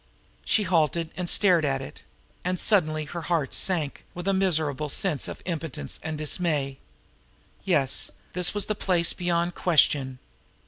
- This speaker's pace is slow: No, average, 145 wpm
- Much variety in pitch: No, average, 3.3 semitones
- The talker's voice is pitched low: No, medium, 165 Hz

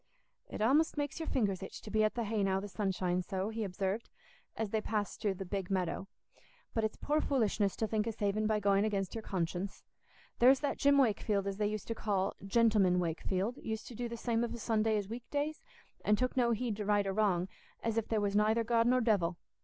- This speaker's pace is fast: Yes, fast, 230 wpm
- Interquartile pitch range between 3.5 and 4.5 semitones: No, average, 2.8 semitones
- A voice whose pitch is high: Yes, high, 215 Hz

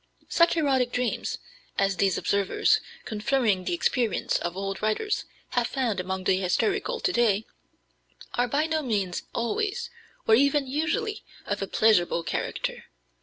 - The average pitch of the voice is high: Yes, high, 235 Hz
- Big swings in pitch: Yes, wide, 7.8 semitones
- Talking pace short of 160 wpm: Yes, average, 140 wpm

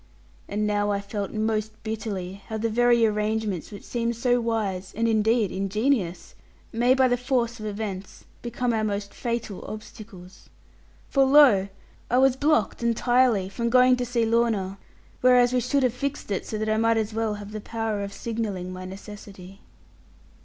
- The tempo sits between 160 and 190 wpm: Yes, average, 170 wpm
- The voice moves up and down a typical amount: Yes, average, 3.0 semitones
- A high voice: Yes, high, 220 Hz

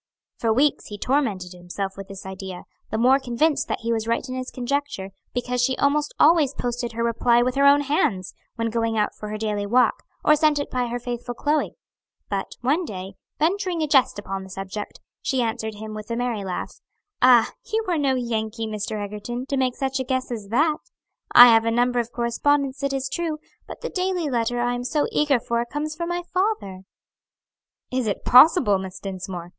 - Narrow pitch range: No, average, 4.6 semitones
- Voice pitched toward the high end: Yes, high, 245 Hz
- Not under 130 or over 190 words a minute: No, fast, 205 wpm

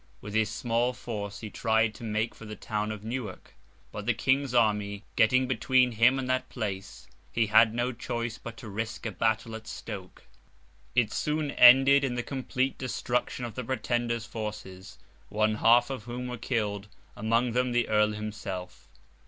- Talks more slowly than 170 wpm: No, average, 175 wpm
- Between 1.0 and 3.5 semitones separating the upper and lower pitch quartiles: Yes, narrow, 2.6 semitones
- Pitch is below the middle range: Yes, low, 115 Hz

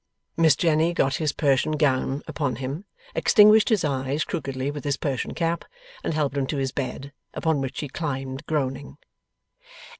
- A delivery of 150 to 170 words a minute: Yes, average, 160 wpm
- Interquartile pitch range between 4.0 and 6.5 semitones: No, average, 2.8 semitones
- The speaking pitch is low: No, medium, 145 Hz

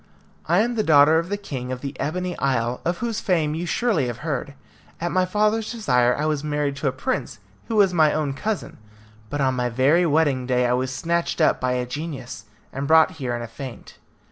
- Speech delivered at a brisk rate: Yes, fast, 220 wpm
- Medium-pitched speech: Yes, medium, 150 Hz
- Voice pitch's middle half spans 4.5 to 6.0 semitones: Yes, average, 5.1 semitones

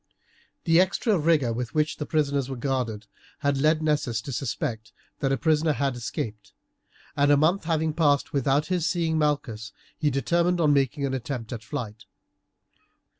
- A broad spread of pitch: No, average, 4.0 semitones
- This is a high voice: No, medium, 145 Hz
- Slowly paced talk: No, average, 165 wpm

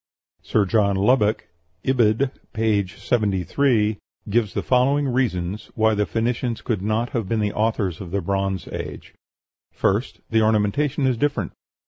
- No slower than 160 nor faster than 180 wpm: No, average, 140 wpm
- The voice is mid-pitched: No, low, 110 Hz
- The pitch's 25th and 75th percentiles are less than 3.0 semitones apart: No, average, 3.4 semitones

